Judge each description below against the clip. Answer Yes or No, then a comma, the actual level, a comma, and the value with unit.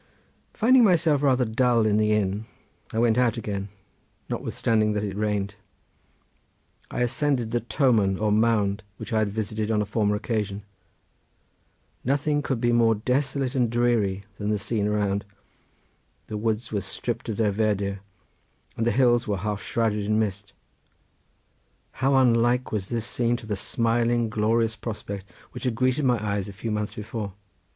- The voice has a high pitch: No, low, 110 Hz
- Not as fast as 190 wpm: Yes, average, 160 wpm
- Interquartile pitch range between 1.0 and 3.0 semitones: Yes, narrow, 2.6 semitones